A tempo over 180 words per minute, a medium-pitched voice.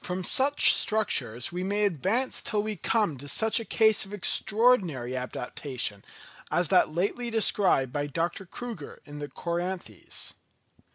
No: average, 145 wpm; medium, 180 Hz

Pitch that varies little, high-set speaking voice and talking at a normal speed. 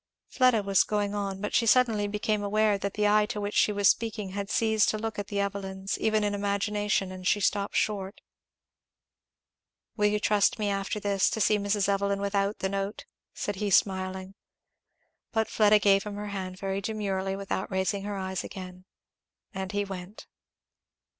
Yes: narrow, 1.2 semitones; high, 200 Hz; average, 180 wpm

